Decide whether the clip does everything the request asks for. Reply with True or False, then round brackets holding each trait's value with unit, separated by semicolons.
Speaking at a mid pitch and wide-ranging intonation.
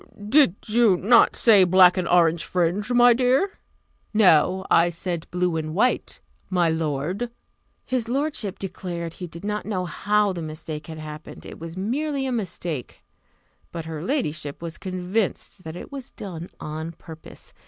False (180 Hz; 4.9 semitones)